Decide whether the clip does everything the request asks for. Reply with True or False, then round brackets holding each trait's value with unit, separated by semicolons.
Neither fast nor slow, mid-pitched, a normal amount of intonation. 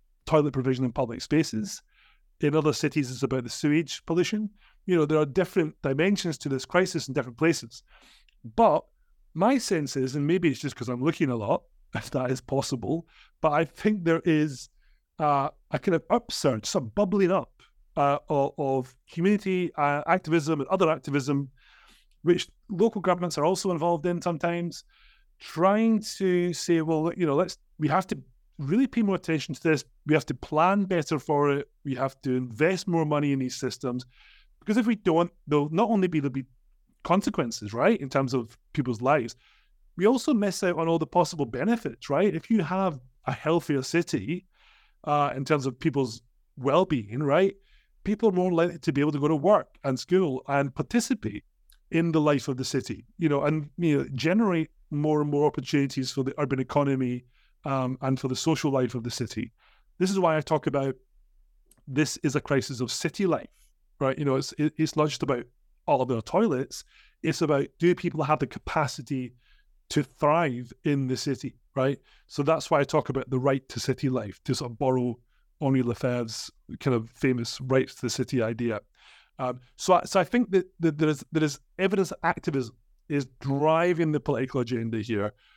True (190 wpm; 150 Hz; 4.5 semitones)